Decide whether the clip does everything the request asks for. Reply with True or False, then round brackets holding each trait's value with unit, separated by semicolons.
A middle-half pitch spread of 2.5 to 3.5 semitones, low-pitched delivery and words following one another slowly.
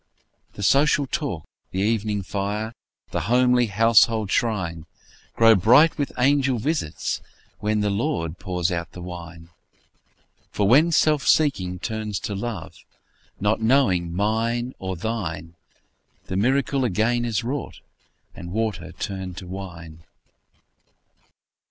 False (4.8 semitones; 105 Hz; 120 wpm)